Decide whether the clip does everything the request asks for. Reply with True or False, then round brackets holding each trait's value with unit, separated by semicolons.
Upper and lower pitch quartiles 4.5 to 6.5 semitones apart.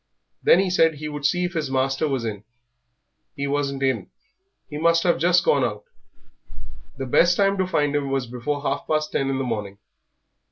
False (3.6 semitones)